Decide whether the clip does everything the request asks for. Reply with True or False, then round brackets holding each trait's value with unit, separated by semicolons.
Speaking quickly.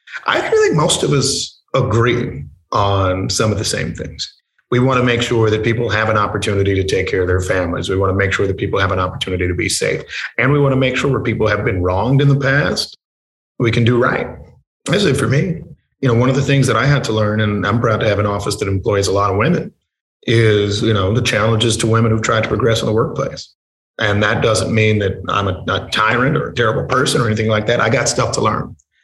True (255 wpm)